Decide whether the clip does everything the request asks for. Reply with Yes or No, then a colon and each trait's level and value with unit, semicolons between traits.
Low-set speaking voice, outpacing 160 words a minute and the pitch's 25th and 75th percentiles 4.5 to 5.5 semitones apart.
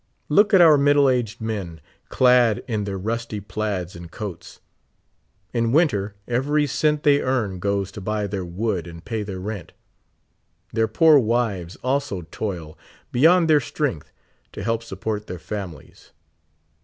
No: low, 110 Hz; average, 145 wpm; average, 5.1 semitones